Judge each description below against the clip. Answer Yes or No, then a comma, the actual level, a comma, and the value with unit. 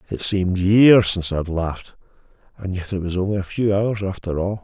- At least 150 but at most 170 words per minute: No, fast, 205 wpm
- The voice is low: Yes, very low, 95 Hz